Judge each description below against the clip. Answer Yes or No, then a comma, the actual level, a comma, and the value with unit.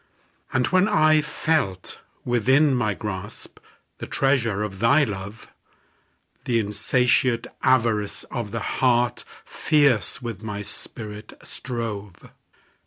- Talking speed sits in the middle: No, slow, 105 wpm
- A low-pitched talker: Yes, low, 115 Hz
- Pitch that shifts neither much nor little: Yes, average, 3.9 semitones